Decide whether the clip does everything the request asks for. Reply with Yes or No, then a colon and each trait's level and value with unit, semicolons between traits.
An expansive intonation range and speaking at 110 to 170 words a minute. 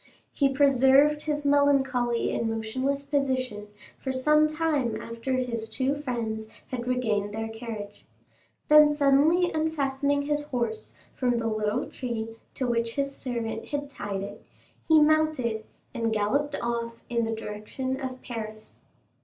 No: average, 4.1 semitones; slow, 135 wpm